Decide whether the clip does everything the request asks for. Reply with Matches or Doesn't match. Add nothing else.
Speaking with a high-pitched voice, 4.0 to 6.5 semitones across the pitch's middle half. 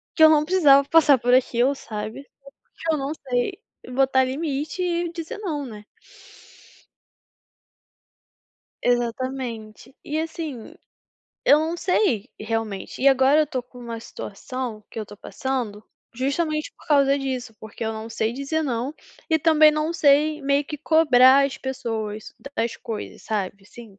Matches